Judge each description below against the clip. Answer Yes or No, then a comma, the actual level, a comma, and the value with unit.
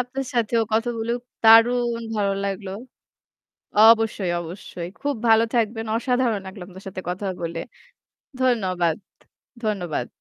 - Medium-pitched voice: No, high, 220 Hz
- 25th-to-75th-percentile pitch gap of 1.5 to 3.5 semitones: No, average, 3.9 semitones